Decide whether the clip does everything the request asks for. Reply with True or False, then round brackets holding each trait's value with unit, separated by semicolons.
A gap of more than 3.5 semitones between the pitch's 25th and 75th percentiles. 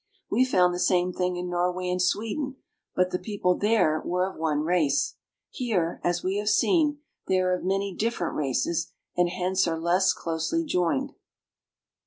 False (2.6 semitones)